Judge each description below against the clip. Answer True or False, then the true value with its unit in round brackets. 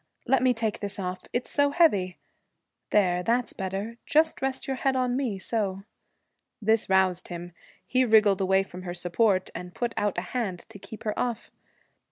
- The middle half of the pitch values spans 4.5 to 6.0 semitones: True (4.8 semitones)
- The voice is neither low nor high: False (210 Hz)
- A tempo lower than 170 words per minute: False (180 wpm)